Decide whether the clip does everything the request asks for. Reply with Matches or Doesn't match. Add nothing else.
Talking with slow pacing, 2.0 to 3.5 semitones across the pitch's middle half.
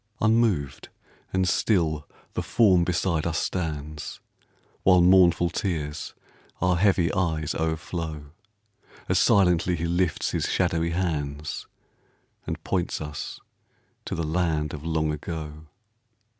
Matches